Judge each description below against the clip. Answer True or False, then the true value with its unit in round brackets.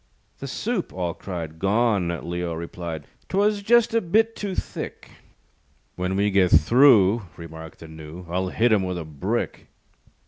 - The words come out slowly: False (150 wpm)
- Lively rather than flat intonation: True (6.1 semitones)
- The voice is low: True (95 Hz)